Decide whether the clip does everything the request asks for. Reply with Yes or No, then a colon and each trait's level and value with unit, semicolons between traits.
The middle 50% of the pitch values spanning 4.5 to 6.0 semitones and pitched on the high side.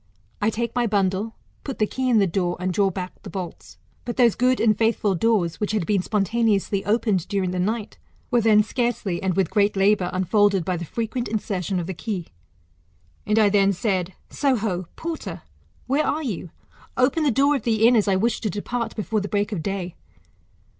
No: average, 3.6 semitones; high, 210 Hz